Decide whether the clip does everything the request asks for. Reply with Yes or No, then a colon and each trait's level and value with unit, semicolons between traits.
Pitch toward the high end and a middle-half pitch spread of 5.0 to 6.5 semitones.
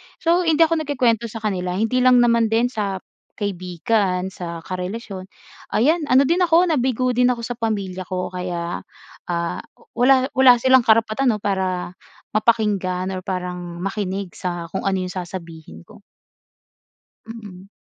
Yes: high, 210 Hz; wide, 5.4 semitones